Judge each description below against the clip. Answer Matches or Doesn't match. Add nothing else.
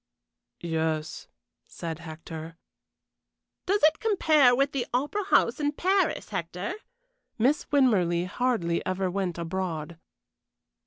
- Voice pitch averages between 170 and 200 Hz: Matches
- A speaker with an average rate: Doesn't match